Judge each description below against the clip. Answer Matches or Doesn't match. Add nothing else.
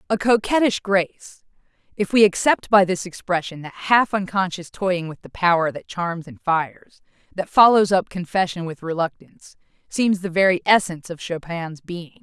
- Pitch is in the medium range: Matches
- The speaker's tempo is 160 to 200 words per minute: Doesn't match